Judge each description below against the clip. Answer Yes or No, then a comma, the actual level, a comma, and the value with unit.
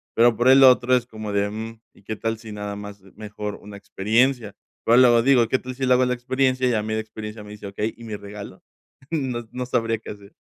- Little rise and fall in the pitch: No, average, 3.2 semitones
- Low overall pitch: Yes, low, 115 Hz